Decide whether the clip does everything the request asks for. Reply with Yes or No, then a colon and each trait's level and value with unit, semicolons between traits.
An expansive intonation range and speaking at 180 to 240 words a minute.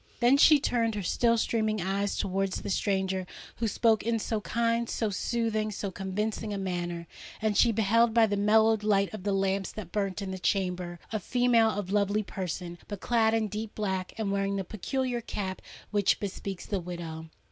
No: average, 2.7 semitones; average, 190 wpm